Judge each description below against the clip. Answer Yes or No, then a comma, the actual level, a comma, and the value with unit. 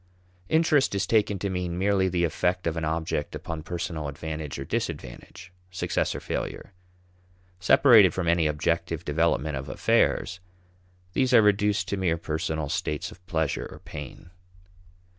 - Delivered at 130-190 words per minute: Yes, average, 145 wpm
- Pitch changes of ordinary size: Yes, average, 3.5 semitones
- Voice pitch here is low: Yes, very low, 85 Hz